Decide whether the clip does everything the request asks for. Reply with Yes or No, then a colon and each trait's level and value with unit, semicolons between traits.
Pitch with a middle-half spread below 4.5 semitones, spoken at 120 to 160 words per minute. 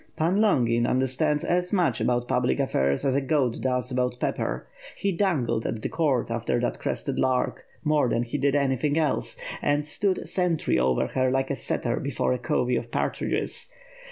No: average, 4.0 semitones; average, 180 wpm